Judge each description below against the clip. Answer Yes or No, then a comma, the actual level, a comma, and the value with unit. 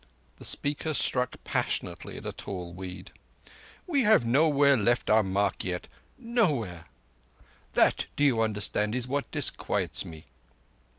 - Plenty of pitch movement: Yes, wide, 6.7 semitones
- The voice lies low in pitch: Yes, low, 120 Hz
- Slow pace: Yes, slow, 130 wpm